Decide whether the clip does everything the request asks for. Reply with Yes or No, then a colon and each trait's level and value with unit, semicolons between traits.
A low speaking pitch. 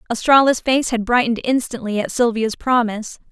No: high, 235 Hz